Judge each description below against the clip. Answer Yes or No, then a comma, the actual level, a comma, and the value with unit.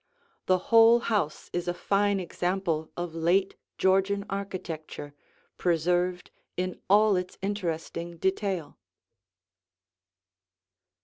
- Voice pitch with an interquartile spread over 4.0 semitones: No, narrow, 2.5 semitones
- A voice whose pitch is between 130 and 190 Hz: Yes, medium, 185 Hz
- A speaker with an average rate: No, slow, 90 wpm